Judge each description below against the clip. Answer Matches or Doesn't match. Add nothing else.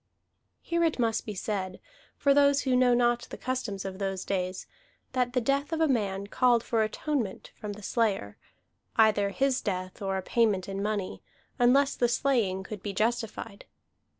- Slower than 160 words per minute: Doesn't match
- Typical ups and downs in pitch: Matches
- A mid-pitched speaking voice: Doesn't match